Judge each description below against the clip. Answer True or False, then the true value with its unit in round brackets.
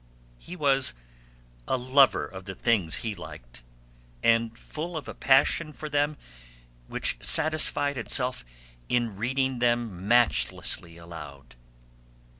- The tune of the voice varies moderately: False (6.7 semitones)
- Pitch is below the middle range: True (120 Hz)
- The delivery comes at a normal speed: False (115 wpm)